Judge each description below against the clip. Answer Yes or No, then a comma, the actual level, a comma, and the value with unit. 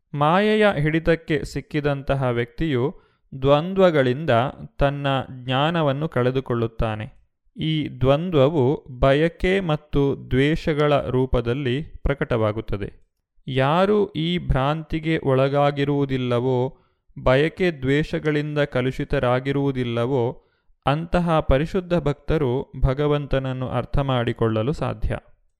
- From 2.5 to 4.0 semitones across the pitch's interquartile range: Yes, average, 3.4 semitones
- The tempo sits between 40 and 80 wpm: Yes, slow, 65 wpm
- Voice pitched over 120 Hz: Yes, medium, 140 Hz